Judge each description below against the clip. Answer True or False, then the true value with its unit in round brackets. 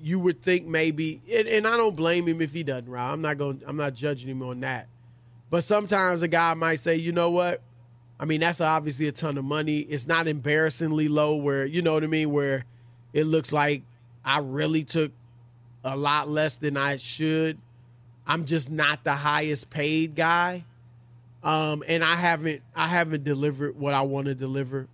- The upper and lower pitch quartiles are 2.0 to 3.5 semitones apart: True (3.0 semitones)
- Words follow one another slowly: False (195 wpm)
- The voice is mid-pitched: True (150 Hz)